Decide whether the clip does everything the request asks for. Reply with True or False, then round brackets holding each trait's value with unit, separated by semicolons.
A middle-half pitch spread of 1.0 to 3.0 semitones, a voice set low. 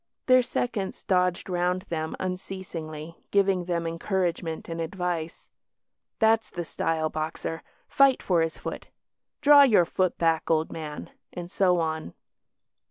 False (2.7 semitones; 175 Hz)